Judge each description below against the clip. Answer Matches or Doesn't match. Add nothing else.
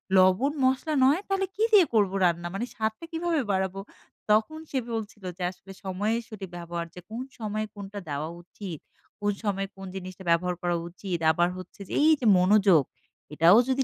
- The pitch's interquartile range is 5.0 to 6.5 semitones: Doesn't match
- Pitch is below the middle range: Doesn't match